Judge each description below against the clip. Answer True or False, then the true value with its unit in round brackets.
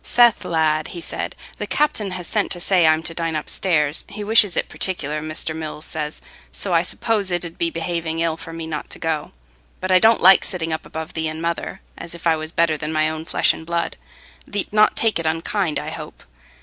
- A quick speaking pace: True (220 wpm)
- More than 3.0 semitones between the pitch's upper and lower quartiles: False (2.6 semitones)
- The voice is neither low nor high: True (165 Hz)